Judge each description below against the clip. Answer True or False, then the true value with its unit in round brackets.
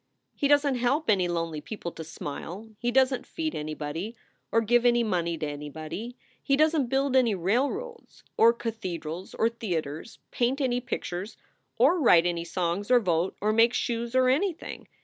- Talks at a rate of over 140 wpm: True (175 wpm)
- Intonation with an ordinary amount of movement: False (6.9 semitones)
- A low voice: False (225 Hz)